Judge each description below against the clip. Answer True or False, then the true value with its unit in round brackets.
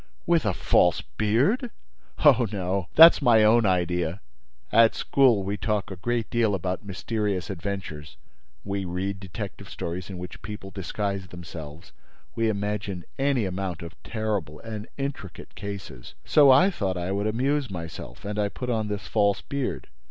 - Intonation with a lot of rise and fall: False (3.9 semitones)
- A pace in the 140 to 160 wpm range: True (155 wpm)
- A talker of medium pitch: False (100 Hz)